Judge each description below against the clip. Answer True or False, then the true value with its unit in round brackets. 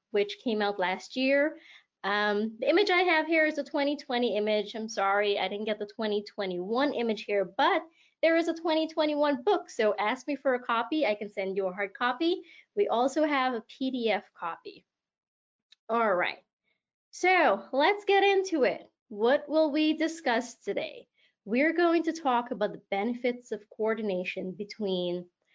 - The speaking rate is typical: True (165 wpm)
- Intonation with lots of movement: True (7.0 semitones)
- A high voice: True (245 Hz)